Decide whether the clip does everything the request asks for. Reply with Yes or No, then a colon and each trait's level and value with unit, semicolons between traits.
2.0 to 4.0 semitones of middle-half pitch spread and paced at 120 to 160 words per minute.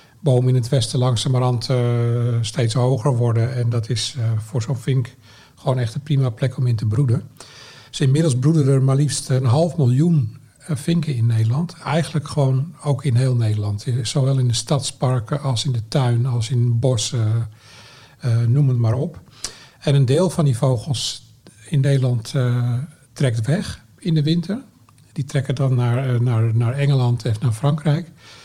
No: average, 3.0 semitones; average, 185 wpm